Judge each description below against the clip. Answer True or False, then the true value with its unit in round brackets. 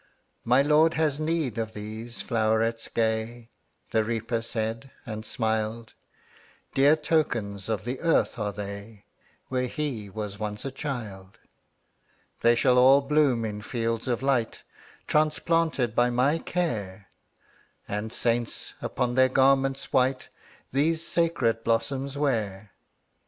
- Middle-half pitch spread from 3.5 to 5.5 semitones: True (3.8 semitones)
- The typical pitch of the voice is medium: False (120 Hz)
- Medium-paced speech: False (125 wpm)